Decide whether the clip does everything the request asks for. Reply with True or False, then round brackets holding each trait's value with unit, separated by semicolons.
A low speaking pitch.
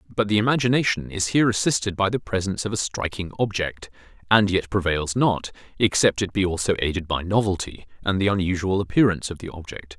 True (95 Hz)